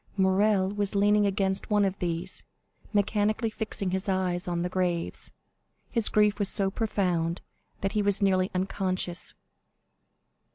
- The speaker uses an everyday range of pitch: No, narrow, 2.0 semitones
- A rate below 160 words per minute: Yes, slow, 135 wpm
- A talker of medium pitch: No, high, 195 Hz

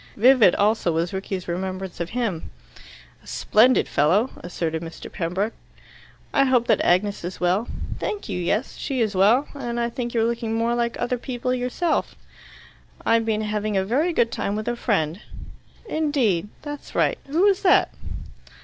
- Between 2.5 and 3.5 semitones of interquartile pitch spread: No, average, 4.9 semitones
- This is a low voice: No, high, 225 Hz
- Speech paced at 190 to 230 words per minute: No, average, 165 wpm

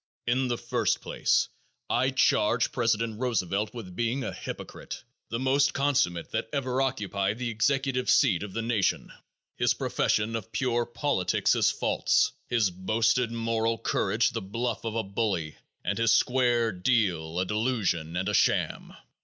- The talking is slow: No, average, 155 wpm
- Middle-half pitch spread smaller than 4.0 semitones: Yes, average, 3.3 semitones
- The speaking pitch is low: Yes, low, 115 Hz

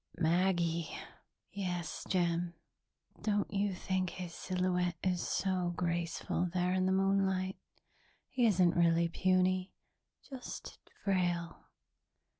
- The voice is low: No, medium, 180 Hz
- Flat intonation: Yes, narrow, 1.6 semitones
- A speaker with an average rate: No, slow, 100 wpm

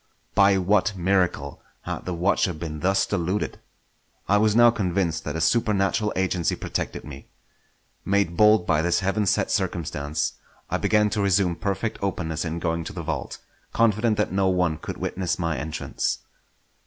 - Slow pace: No, average, 160 wpm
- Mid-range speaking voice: No, very low, 95 Hz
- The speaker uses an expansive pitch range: No, average, 3.4 semitones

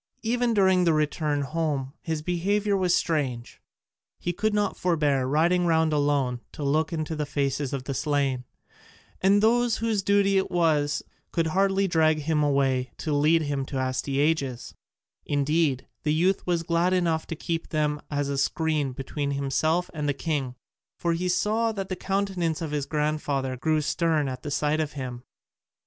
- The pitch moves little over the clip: No, average, 3.7 semitones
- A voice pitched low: No, medium, 155 Hz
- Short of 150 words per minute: No, average, 170 wpm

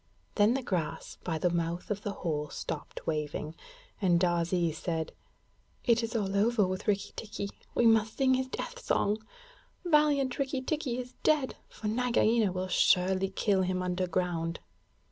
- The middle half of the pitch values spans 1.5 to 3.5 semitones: No, average, 5.1 semitones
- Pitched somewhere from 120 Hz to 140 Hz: No, high, 200 Hz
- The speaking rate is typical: Yes, average, 155 wpm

